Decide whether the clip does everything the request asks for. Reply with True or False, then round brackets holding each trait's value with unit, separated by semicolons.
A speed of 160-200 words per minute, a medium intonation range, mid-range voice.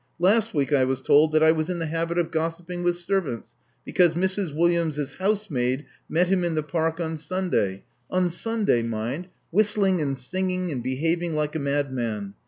True (190 wpm; 4.1 semitones; 165 Hz)